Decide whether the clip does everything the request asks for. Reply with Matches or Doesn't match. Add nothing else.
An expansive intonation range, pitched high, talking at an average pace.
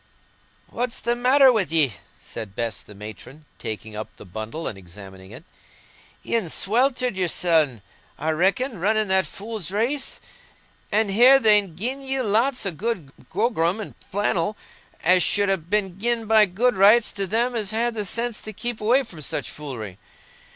Matches